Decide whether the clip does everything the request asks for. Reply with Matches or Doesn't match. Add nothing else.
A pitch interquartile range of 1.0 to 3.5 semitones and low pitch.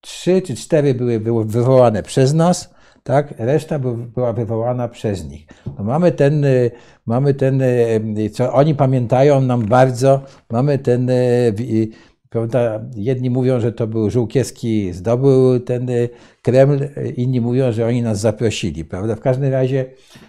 Matches